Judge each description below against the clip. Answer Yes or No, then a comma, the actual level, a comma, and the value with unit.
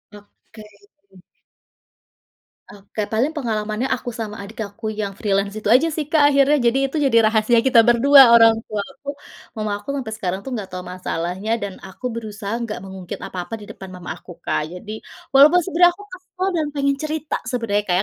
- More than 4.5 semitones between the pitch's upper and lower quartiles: Yes, average, 5.2 semitones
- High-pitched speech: Yes, high, 225 Hz